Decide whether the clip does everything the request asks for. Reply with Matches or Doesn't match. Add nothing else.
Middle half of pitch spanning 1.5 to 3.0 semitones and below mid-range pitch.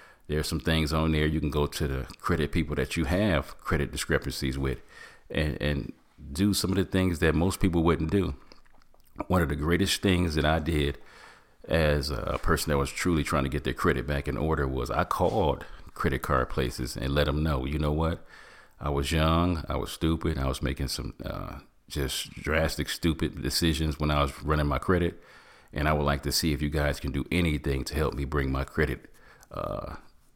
Matches